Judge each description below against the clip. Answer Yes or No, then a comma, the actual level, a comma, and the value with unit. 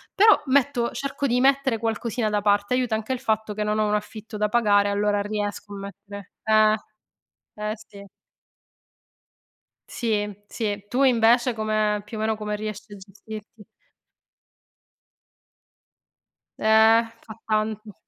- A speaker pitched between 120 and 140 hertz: No, high, 215 Hz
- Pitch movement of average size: No, narrow, 1.8 semitones